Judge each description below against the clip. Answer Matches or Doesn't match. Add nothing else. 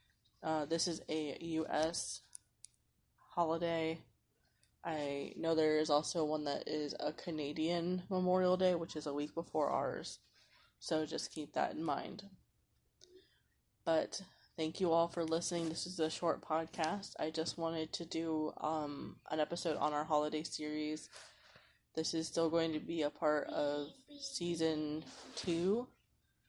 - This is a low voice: Doesn't match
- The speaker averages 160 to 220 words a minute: Doesn't match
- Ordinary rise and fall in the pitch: Doesn't match